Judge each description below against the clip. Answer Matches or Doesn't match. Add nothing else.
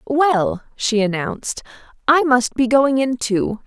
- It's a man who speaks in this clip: Doesn't match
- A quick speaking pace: Doesn't match